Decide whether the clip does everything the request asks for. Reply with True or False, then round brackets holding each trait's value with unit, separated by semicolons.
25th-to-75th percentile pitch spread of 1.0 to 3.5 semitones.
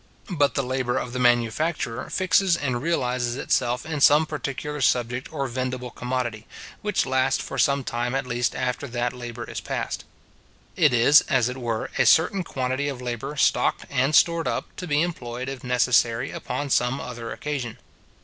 True (2.9 semitones)